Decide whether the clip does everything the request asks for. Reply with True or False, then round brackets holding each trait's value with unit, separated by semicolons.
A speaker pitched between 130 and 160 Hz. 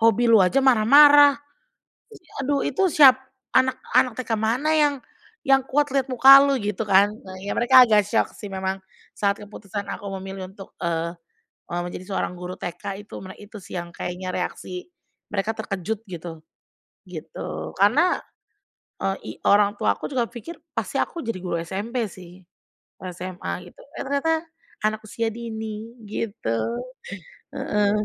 False (215 Hz)